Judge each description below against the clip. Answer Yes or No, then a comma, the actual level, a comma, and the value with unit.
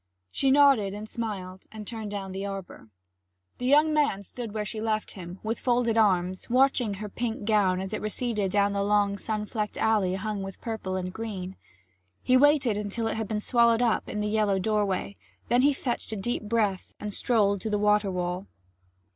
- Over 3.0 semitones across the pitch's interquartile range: No, average, 2.7 semitones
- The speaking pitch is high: Yes, high, 210 Hz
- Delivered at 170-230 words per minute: Yes, average, 195 wpm